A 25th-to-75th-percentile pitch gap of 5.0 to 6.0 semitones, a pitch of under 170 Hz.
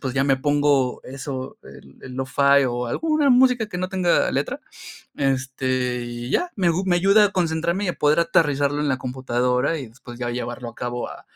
Yes: wide, 5.5 semitones; medium, 140 Hz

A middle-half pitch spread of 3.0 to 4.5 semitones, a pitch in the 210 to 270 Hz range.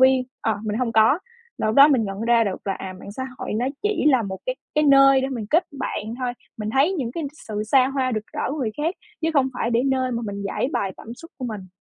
Yes: average, 4.0 semitones; very high, 250 Hz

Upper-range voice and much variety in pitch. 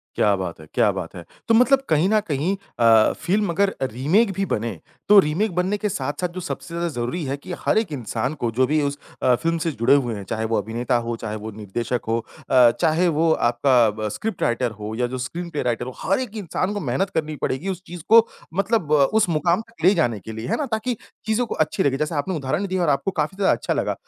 No: medium, 150 Hz; wide, 7.8 semitones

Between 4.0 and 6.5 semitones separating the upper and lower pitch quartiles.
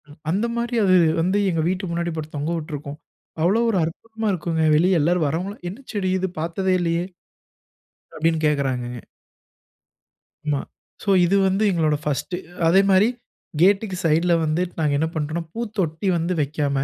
No: average, 3.6 semitones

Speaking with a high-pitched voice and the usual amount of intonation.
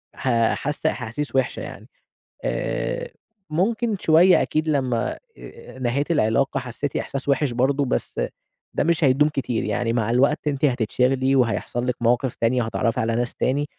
No: low, 135 Hz; average, 3.5 semitones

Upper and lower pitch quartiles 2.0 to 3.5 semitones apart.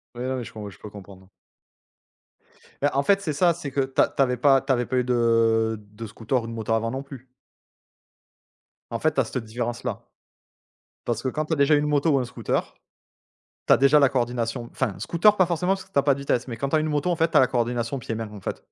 No: average, 4.0 semitones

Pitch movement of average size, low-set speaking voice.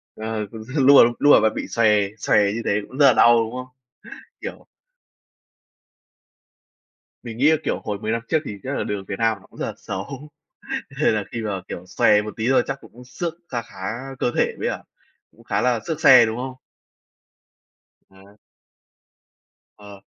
Yes: average, 3.8 semitones; low, 115 Hz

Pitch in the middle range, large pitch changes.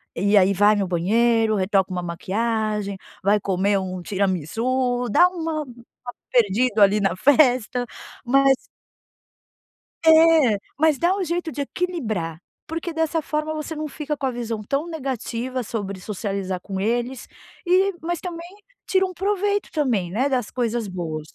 No: high, 240 Hz; wide, 7.5 semitones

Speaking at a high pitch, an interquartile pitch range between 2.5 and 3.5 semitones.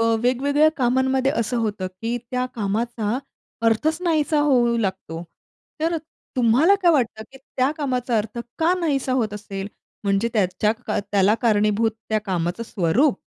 No: high, 230 Hz; average, 4.2 semitones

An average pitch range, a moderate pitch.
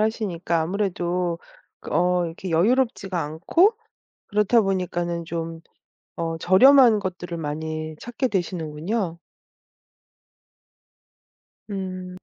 Yes: average, 3.6 semitones; medium, 180 Hz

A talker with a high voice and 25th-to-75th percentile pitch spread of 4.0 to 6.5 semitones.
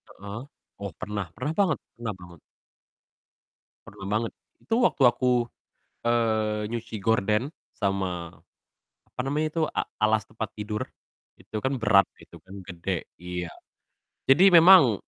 No: low, 110 Hz; average, 4.3 semitones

